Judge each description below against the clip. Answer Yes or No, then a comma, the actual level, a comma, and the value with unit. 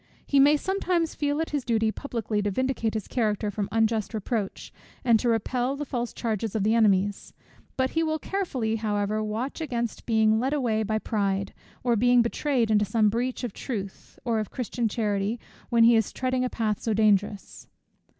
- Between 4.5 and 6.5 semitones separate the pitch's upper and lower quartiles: No, average, 3.1 semitones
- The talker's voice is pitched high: Yes, high, 225 Hz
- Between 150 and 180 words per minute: No, average, 190 wpm